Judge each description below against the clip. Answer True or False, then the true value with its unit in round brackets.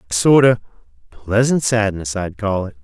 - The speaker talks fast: False (170 wpm)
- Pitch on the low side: True (105 Hz)